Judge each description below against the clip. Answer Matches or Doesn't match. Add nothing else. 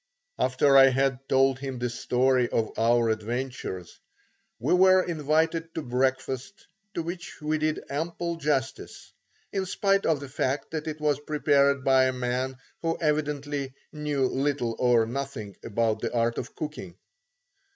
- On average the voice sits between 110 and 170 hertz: Matches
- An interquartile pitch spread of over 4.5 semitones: Doesn't match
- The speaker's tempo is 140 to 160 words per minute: Matches